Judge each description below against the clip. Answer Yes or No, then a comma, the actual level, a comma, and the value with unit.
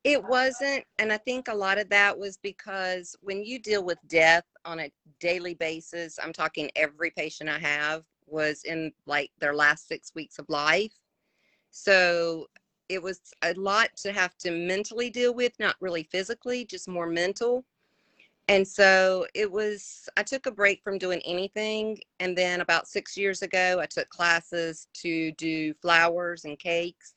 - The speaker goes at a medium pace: Yes, average, 170 wpm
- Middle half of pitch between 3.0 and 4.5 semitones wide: Yes, average, 3.5 semitones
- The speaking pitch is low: No, medium, 180 Hz